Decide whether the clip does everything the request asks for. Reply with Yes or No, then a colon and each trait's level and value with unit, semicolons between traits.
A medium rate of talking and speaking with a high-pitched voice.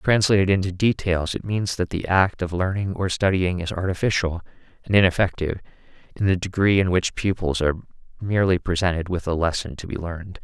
No: average, 180 wpm; very low, 90 Hz